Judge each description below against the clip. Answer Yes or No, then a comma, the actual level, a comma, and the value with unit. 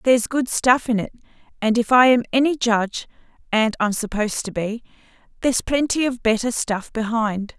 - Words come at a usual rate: Yes, average, 175 wpm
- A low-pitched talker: No, high, 230 Hz